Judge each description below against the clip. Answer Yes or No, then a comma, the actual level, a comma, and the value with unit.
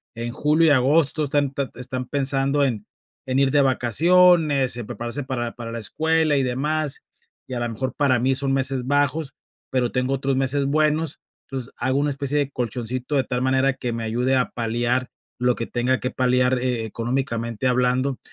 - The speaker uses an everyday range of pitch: No, narrow, 2.3 semitones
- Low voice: Yes, low, 130 Hz